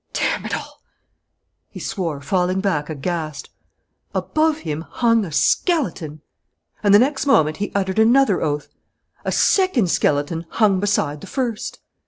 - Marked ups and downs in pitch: Yes, wide, 6.8 semitones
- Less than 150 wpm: Yes, average, 140 wpm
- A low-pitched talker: No, high, 190 Hz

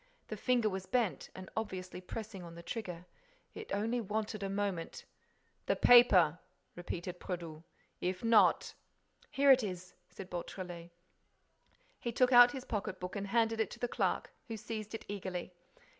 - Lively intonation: No, average, 4.0 semitones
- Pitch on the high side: Yes, high, 200 Hz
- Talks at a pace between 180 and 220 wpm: No, average, 160 wpm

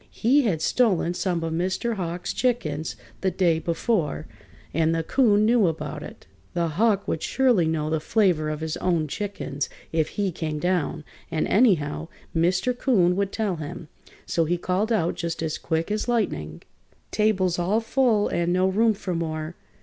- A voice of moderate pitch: Yes, medium, 175 Hz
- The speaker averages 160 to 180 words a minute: Yes, average, 170 wpm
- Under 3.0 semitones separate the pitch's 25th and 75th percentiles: No, average, 4.6 semitones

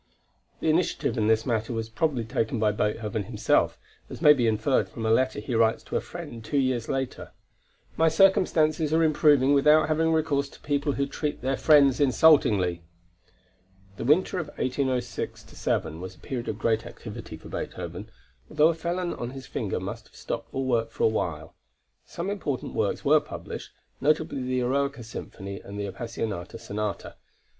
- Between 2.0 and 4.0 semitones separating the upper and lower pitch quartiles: No, average, 5.2 semitones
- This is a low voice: Yes, low, 130 Hz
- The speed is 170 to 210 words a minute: Yes, average, 175 wpm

